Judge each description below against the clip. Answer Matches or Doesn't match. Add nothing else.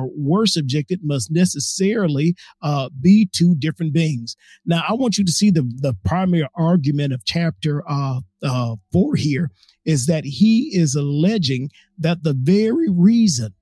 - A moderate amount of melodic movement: Matches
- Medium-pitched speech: Matches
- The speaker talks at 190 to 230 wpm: Doesn't match